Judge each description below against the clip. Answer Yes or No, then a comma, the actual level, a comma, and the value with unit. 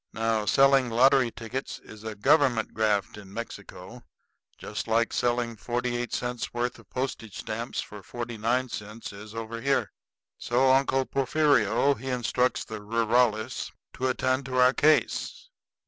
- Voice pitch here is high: No, low, 120 Hz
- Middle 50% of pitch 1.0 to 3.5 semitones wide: Yes, average, 2.7 semitones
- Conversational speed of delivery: Yes, average, 145 wpm